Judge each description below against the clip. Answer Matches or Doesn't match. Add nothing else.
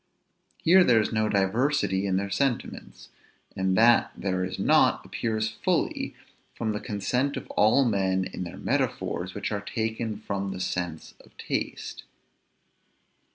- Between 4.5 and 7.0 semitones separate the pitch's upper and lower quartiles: Doesn't match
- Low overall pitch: Matches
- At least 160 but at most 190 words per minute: Doesn't match